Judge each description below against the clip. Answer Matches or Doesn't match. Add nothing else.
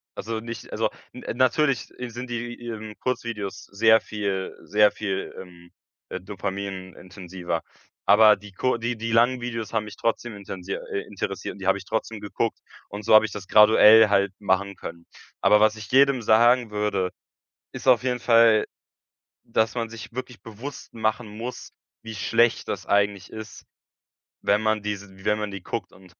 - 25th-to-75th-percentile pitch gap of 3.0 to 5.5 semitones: Doesn't match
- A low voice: Matches